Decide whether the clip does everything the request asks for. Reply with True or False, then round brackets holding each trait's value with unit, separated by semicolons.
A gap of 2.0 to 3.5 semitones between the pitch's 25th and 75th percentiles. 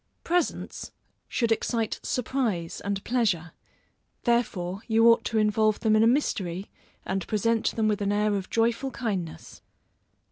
True (2.9 semitones)